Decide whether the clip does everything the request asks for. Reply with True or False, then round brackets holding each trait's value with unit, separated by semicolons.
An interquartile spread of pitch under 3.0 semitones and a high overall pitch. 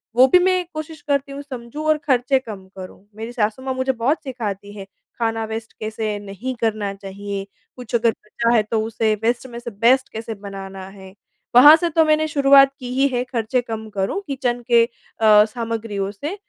False (4.0 semitones; 235 Hz)